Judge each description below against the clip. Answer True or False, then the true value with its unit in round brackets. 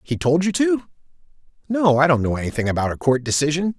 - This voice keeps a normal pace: True (175 wpm)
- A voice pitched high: False (150 Hz)